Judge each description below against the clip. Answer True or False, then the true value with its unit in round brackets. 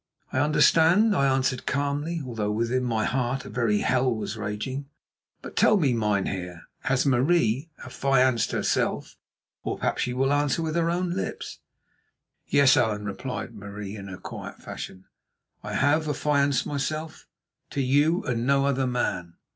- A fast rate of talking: False (145 wpm)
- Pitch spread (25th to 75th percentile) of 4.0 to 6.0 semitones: True (4.5 semitones)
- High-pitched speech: False (130 Hz)